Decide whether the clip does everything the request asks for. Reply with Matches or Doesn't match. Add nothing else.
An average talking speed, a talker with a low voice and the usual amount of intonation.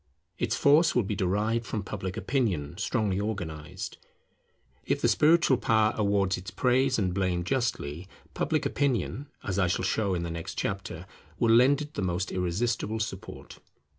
Matches